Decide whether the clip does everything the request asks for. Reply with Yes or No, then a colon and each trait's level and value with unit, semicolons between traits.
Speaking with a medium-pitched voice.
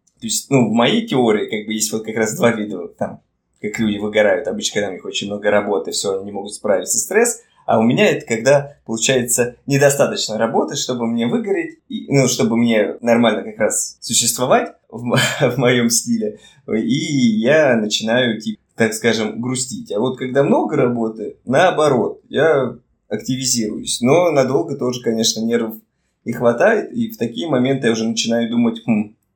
No: low, 120 Hz